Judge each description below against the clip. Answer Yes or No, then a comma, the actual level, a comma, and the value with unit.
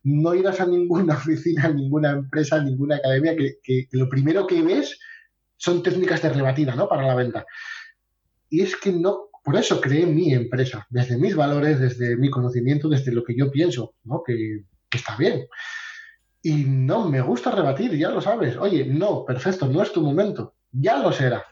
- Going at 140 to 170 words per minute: No, fast, 190 wpm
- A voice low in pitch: No, medium, 145 Hz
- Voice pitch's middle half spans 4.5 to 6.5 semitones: Yes, average, 5.3 semitones